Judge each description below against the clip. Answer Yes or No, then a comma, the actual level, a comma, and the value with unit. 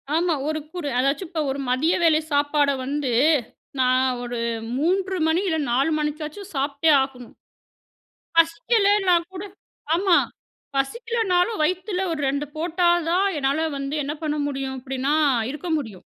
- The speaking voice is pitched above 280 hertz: Yes, very high, 310 Hz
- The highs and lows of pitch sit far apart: No, average, 4.6 semitones